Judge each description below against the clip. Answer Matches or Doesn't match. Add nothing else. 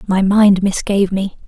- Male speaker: Doesn't match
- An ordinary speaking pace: Matches